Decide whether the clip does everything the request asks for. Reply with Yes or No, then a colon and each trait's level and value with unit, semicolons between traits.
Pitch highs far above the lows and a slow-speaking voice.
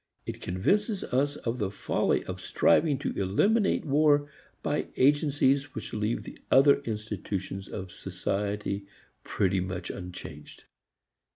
Yes: wide, 6.9 semitones; slow, 115 wpm